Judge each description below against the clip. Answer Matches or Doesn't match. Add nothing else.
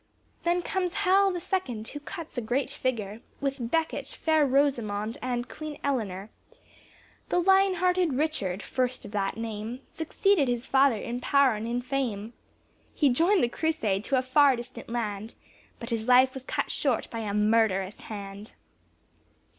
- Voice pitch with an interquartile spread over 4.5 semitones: Matches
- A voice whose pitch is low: Doesn't match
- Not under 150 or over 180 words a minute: Matches